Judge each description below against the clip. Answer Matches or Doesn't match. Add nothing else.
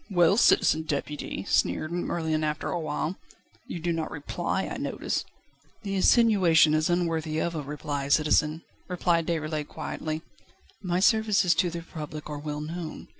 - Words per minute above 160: Doesn't match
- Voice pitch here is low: Doesn't match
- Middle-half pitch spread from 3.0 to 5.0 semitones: Doesn't match